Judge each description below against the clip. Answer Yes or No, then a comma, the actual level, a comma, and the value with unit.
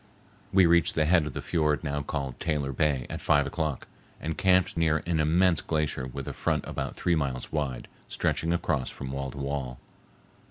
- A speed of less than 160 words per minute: No, average, 190 wpm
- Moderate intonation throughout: Yes, average, 3.1 semitones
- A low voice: Yes, very low, 75 Hz